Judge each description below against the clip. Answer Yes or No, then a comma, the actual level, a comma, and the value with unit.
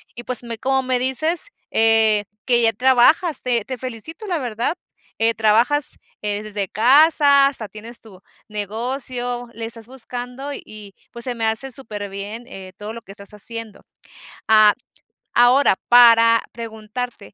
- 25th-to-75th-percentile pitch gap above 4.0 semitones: No, average, 2.9 semitones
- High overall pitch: Yes, high, 235 Hz